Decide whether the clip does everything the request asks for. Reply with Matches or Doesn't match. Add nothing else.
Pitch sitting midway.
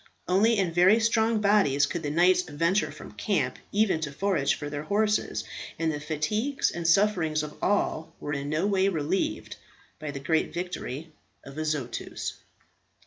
Matches